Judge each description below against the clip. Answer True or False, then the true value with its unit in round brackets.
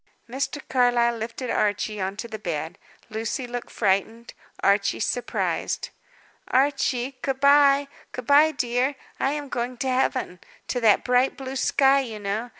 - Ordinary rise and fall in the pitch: True (3.5 semitones)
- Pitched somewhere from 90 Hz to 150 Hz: False (245 Hz)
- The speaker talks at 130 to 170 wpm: True (150 wpm)